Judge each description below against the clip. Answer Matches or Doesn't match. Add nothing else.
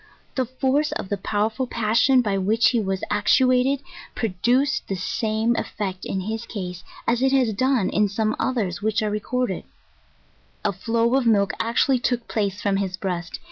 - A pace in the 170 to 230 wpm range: Matches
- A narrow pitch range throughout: Doesn't match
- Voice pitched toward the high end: Matches